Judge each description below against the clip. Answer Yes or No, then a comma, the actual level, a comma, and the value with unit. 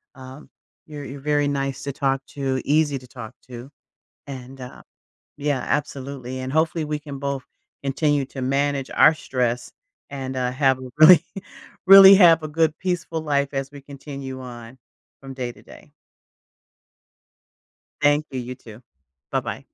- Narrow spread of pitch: Yes, narrow, 2.2 semitones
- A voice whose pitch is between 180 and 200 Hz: No, medium, 140 Hz